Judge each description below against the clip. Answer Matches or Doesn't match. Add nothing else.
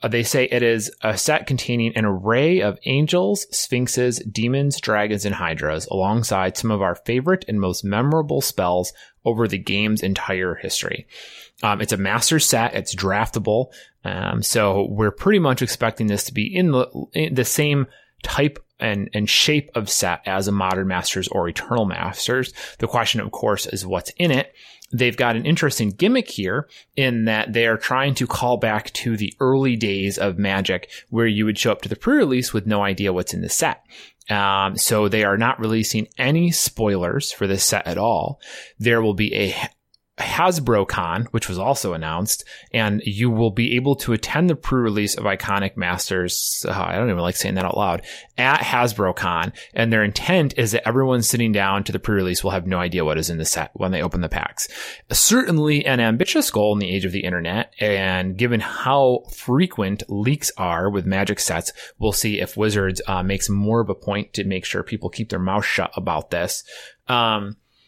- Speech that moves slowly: Doesn't match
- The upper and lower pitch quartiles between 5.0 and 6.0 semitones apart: Doesn't match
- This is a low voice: Matches